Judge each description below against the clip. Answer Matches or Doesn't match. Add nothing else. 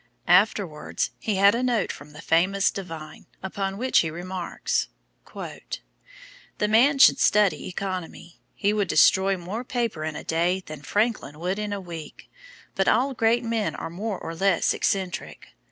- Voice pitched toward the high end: Matches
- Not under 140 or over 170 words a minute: Matches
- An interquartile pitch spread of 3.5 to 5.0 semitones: Matches